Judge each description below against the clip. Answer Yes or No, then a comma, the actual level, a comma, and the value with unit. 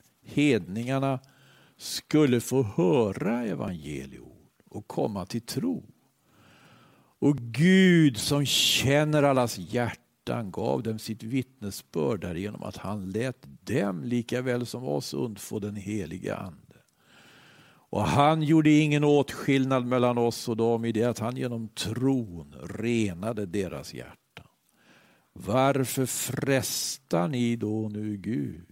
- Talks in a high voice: No, low, 120 Hz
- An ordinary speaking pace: No, slow, 115 wpm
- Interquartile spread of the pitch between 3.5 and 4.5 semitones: Yes, average, 4.2 semitones